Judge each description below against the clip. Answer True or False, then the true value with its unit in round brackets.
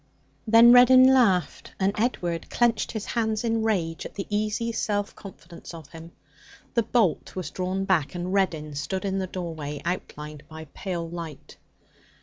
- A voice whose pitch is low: False (190 Hz)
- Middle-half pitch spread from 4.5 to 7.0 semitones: True (4.9 semitones)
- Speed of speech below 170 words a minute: True (155 wpm)